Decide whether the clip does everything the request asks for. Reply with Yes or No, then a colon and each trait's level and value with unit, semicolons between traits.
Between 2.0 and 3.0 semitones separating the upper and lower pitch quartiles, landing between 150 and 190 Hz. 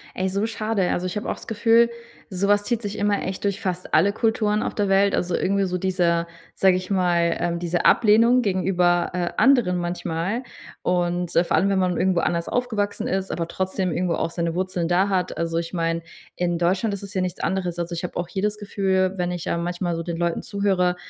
Yes: narrow, 2.4 semitones; medium, 185 Hz